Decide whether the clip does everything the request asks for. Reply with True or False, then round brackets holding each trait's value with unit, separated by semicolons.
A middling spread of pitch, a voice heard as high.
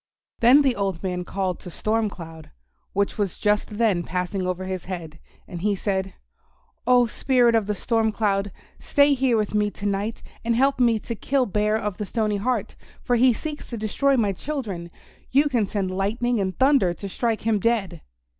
True (3.7 semitones; 210 Hz)